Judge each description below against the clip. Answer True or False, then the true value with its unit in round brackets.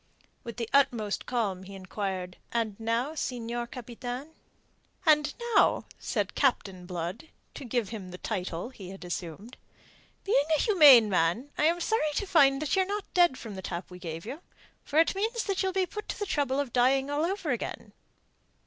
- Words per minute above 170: True (185 wpm)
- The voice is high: True (245 Hz)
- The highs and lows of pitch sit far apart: True (7.6 semitones)